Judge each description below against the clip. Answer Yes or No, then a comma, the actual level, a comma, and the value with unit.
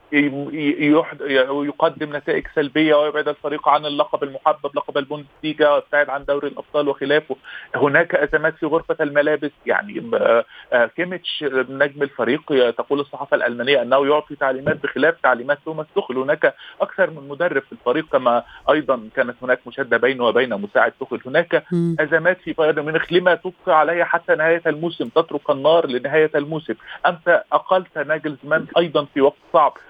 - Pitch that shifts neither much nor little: No, narrow, 1.9 semitones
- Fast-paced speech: Yes, fast, 140 wpm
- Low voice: No, medium, 150 Hz